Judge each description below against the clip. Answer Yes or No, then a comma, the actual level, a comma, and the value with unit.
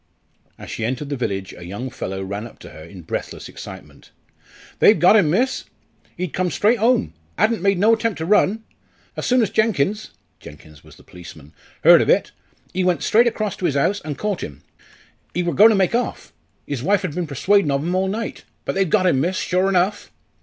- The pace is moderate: No, fast, 210 wpm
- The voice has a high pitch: No, medium, 180 Hz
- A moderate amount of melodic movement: No, wide, 7.9 semitones